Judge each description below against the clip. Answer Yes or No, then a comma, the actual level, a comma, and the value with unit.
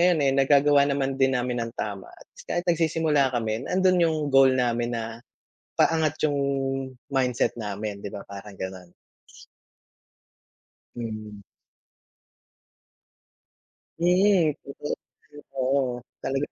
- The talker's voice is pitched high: No, low, 135 Hz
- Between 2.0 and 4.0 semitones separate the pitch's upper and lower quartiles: No, average, 4.8 semitones